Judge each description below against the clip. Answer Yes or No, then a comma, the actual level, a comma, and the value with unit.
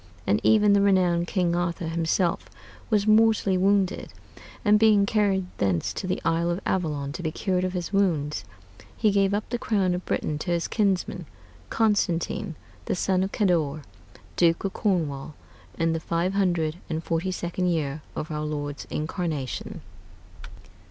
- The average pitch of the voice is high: No, medium, 180 Hz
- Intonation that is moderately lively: Yes, average, 3.5 semitones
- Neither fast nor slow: Yes, average, 160 wpm